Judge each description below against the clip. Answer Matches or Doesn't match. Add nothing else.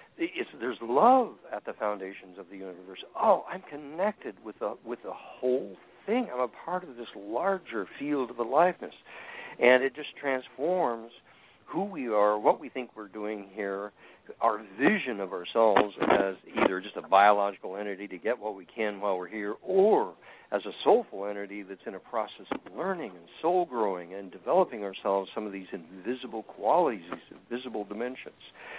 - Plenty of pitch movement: Matches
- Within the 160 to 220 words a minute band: Matches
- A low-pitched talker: Matches